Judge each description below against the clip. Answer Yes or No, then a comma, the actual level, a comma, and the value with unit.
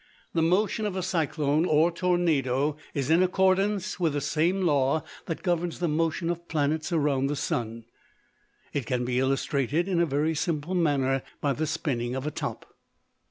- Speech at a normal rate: Yes, average, 170 wpm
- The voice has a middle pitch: Yes, medium, 155 Hz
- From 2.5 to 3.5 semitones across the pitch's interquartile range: No, average, 3.9 semitones